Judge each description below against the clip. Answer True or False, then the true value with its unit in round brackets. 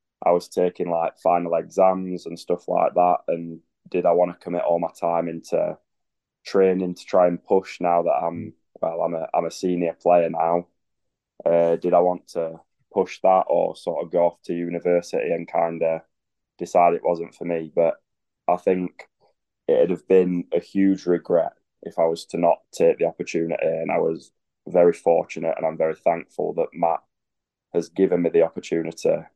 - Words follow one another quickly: False (190 wpm)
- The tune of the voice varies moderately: False (1.3 semitones)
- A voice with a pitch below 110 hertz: True (85 Hz)